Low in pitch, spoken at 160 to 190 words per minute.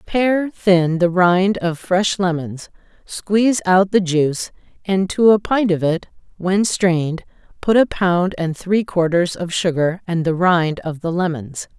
No: medium, 180 Hz; average, 170 wpm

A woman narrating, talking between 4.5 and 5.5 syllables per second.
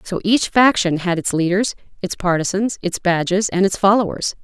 Yes: female; 5.1 syllables/s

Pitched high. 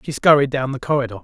No: low, 135 Hz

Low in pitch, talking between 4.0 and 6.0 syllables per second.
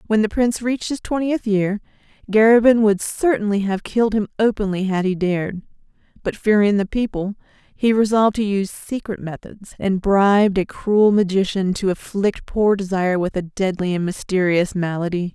No: high, 200 Hz; 5.3 syllables/s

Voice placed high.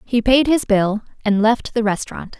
Yes: high, 225 Hz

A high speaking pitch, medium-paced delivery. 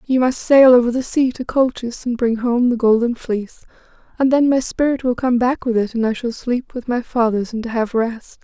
No: high, 240 Hz; fast, 235 wpm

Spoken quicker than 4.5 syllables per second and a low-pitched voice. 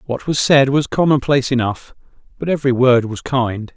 Yes: 5.4 syllables/s; low, 130 Hz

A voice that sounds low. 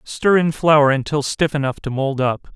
No: medium, 145 Hz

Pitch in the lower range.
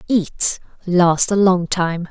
No: medium, 180 Hz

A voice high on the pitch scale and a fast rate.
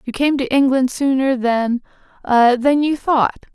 No: very high, 260 Hz; slow, 135 wpm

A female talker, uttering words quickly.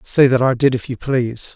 No: male; fast, 270 wpm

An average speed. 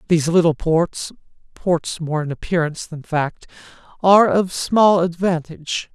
No: slow, 130 wpm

